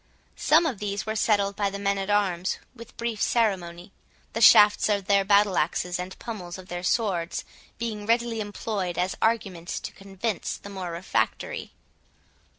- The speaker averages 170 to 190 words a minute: No, average, 160 wpm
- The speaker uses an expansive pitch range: No, average, 2.9 semitones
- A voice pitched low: No, high, 200 Hz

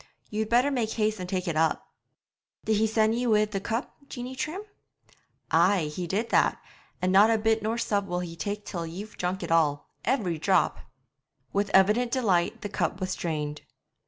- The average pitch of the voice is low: No, high, 205 Hz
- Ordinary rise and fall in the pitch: Yes, average, 3.8 semitones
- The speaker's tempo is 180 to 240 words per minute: Yes, average, 190 wpm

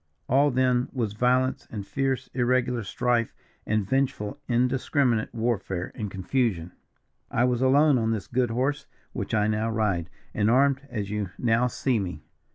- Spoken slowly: No, average, 155 wpm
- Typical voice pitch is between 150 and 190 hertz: No, low, 120 Hz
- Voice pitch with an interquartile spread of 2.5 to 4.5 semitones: Yes, average, 3.4 semitones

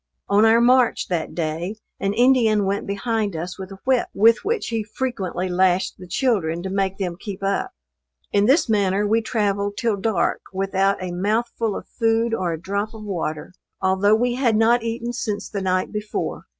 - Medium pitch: No, high, 205 Hz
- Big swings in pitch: No, average, 3.2 semitones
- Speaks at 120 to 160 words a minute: No, average, 185 wpm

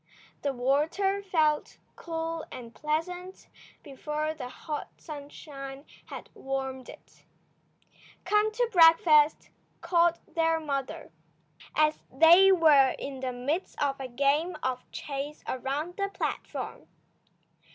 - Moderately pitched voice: No, very high, 300 Hz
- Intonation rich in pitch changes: No, average, 3.6 semitones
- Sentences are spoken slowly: Yes, slow, 110 wpm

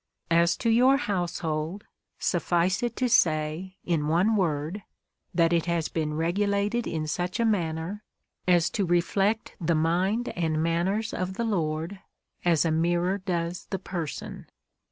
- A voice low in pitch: No, medium, 175 Hz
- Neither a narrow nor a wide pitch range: Yes, average, 3.5 semitones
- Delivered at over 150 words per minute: No, average, 145 wpm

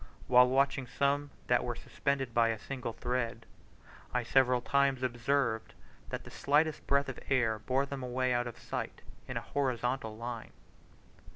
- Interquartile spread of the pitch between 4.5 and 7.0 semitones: No, narrow, 2.5 semitones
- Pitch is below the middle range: Yes, low, 125 Hz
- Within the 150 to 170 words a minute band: Yes, average, 160 wpm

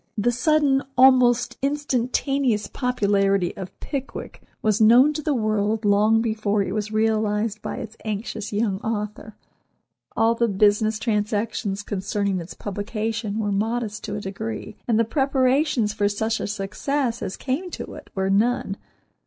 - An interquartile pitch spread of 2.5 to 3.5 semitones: Yes, average, 2.9 semitones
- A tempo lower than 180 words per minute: Yes, average, 145 wpm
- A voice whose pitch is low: No, high, 220 Hz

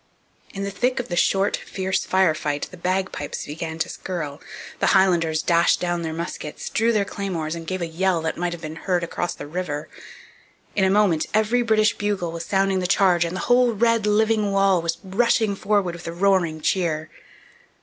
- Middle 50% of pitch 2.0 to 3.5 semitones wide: Yes, average, 3.1 semitones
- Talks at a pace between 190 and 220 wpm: Yes, average, 195 wpm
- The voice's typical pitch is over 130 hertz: Yes, medium, 185 Hz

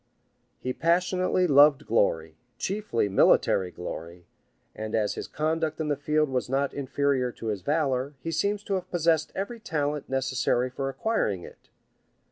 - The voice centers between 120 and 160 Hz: Yes, medium, 140 Hz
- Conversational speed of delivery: Yes, average, 150 wpm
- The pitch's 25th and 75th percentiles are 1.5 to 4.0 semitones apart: No, average, 4.7 semitones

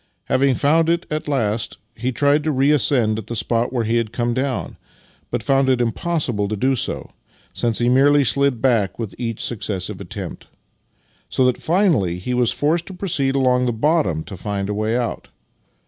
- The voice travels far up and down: No, average, 4.1 semitones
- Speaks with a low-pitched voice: Yes, low, 125 Hz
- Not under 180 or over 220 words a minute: Yes, average, 185 wpm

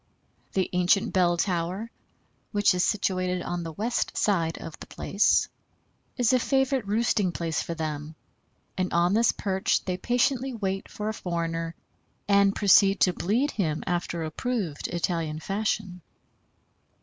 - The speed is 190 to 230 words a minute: No, average, 140 wpm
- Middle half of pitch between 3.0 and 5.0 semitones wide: Yes, average, 3.8 semitones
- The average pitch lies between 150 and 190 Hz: Yes, medium, 185 Hz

